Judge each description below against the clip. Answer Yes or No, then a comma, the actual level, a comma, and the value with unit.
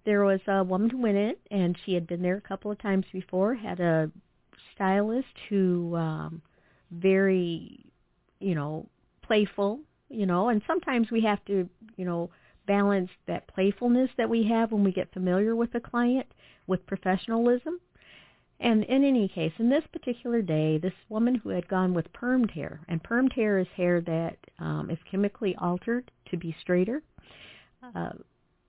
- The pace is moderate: Yes, average, 170 wpm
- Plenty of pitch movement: No, average, 4.3 semitones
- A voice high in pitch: Yes, high, 195 Hz